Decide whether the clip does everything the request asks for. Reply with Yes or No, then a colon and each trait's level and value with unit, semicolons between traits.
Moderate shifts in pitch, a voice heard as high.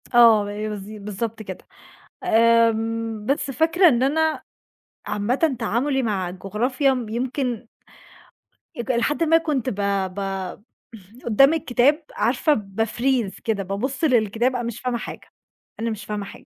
Yes: average, 3.9 semitones; high, 235 Hz